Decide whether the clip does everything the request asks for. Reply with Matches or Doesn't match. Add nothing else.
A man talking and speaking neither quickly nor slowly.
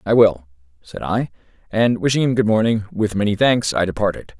Matches